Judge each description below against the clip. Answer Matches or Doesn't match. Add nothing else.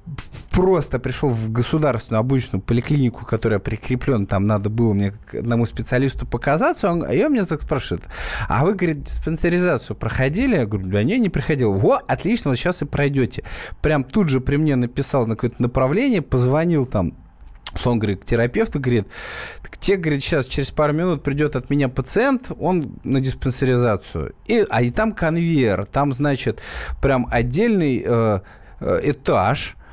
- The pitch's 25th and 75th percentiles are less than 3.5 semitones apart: Doesn't match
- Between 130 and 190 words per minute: Matches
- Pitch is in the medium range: Doesn't match